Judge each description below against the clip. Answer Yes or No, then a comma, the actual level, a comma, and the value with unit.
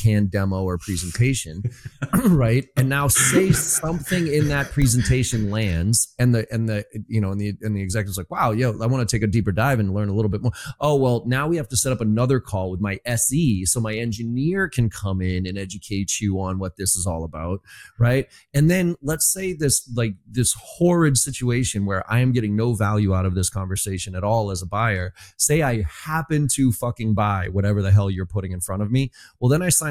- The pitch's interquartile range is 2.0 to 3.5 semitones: No, average, 5.0 semitones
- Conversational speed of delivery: No, fast, 225 wpm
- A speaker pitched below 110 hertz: No, low, 115 Hz